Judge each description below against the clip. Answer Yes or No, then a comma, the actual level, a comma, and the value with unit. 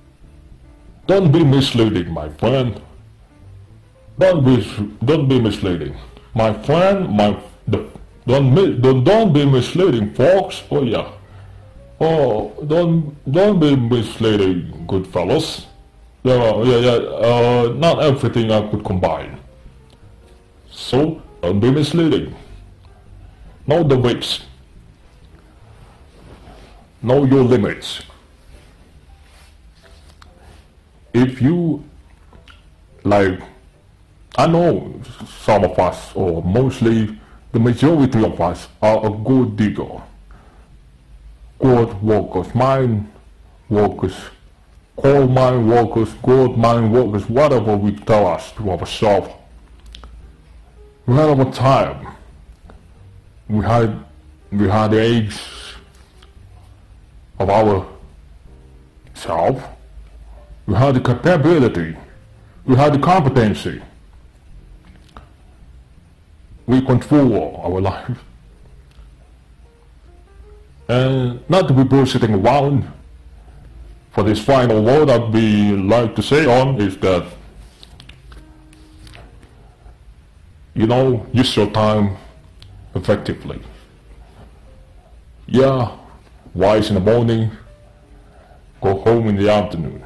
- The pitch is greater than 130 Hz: No, low, 100 Hz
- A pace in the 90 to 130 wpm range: Yes, average, 95 wpm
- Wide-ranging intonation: Yes, wide, 8.1 semitones